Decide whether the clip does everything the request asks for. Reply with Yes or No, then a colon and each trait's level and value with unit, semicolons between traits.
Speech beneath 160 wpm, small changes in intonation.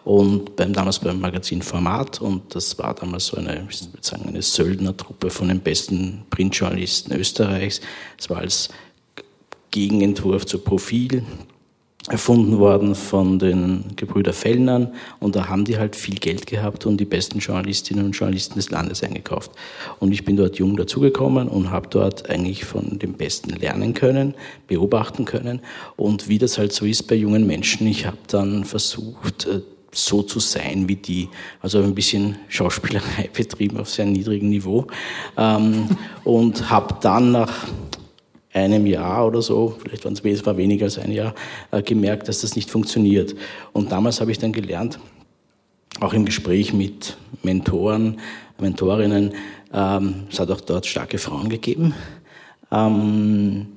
Yes: average, 150 wpm; narrow, 2.3 semitones